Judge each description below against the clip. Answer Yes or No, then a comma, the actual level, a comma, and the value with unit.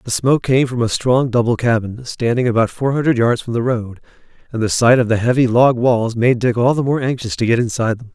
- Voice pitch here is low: Yes, low, 120 Hz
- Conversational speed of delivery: No, fast, 250 wpm